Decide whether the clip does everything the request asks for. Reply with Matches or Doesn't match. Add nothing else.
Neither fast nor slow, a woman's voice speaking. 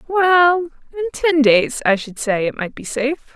Matches